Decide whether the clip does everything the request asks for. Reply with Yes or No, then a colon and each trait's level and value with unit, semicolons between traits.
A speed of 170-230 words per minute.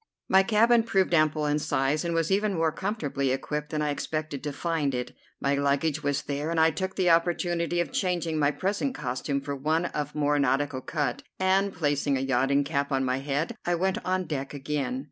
Yes: average, 200 wpm